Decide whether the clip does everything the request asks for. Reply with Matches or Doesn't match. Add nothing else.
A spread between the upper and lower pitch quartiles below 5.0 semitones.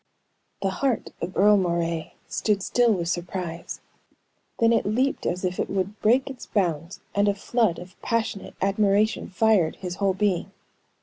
Matches